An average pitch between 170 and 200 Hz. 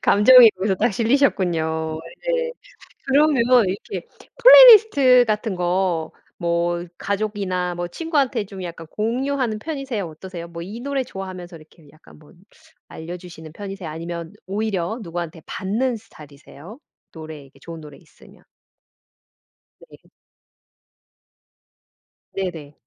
Yes: high, 190 Hz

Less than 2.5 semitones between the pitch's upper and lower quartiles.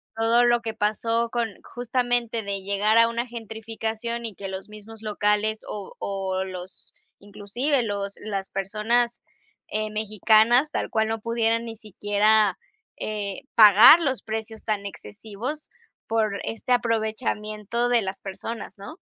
Yes: narrow, 2.1 semitones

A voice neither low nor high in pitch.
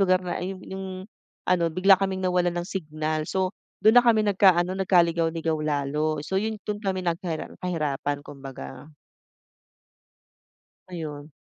Yes: medium, 175 Hz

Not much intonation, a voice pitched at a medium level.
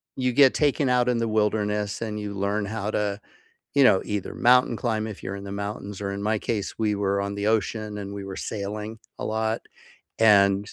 No: narrow, 1.7 semitones; low, 105 Hz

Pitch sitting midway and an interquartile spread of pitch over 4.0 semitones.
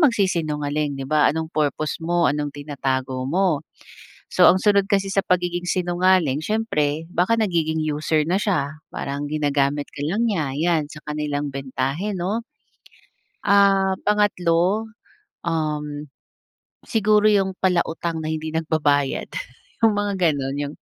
Yes: medium, 160 Hz; average, 4.5 semitones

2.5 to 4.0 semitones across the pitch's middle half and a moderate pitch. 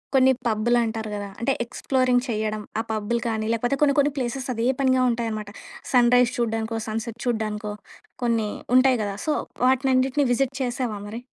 No: average, 2.8 semitones; high, 235 Hz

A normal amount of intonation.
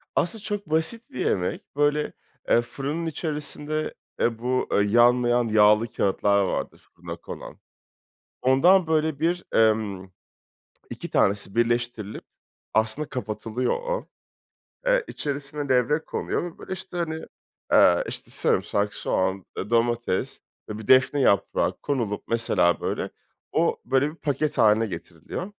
No: wide, 5.9 semitones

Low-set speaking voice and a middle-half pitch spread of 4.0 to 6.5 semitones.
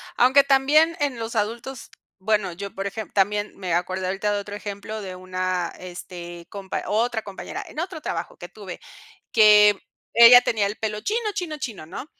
No: high, 210 Hz; average, 4.3 semitones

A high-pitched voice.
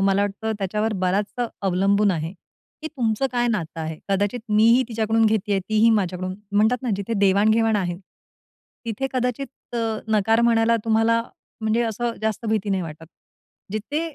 Yes: high, 215 Hz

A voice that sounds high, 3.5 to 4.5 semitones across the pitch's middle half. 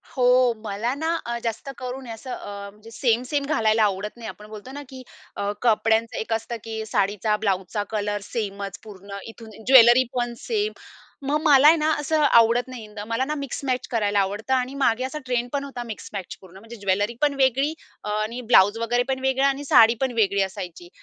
Yes: high, 230 Hz; average, 4.0 semitones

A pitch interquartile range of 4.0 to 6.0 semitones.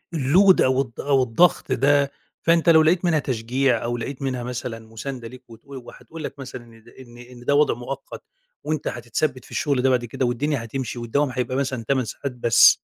No: average, 2.9 semitones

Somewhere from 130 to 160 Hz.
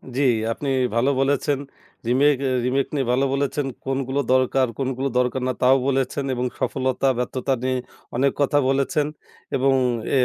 Yes: low, 135 Hz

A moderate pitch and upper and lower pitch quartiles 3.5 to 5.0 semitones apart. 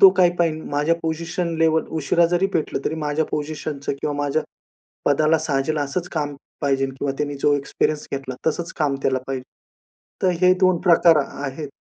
No: medium, 155 Hz; average, 2.7 semitones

